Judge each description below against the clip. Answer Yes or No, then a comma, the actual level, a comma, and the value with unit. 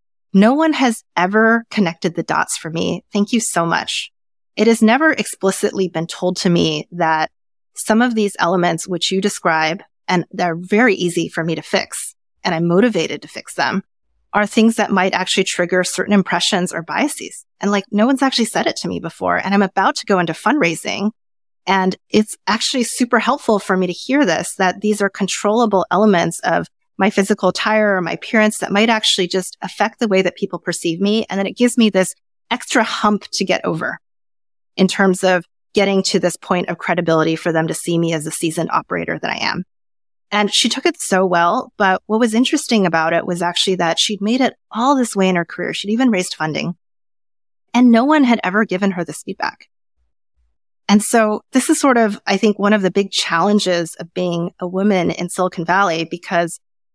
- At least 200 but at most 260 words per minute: Yes, fast, 205 wpm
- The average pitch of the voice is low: No, high, 190 Hz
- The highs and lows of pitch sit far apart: No, average, 3.8 semitones